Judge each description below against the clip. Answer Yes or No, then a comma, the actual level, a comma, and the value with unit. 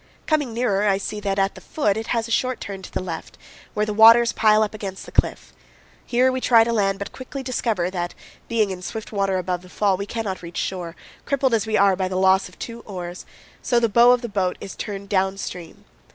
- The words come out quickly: Yes, fast, 240 wpm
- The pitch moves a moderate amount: Yes, average, 3.5 semitones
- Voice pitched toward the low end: No, high, 205 Hz